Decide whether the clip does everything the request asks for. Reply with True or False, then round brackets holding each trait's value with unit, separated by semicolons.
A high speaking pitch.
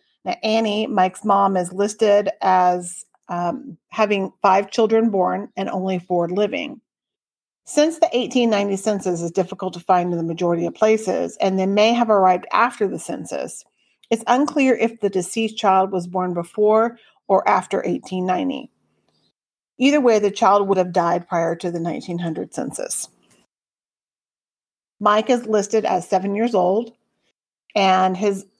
True (195 Hz)